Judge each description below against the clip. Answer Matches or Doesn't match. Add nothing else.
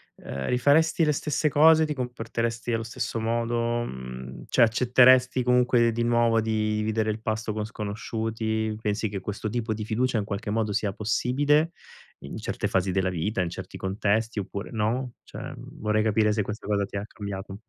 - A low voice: Matches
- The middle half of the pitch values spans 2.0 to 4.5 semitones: Matches